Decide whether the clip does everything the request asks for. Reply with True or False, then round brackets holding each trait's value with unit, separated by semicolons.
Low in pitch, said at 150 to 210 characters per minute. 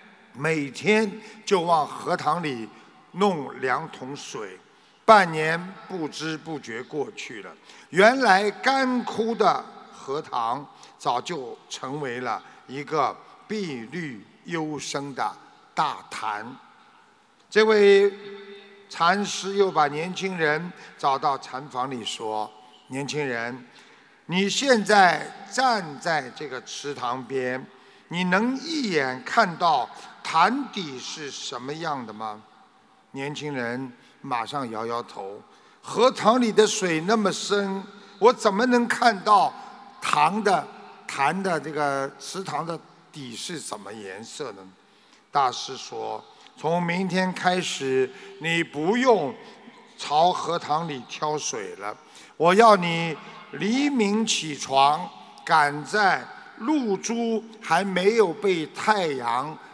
False (185 Hz; 155 characters per minute)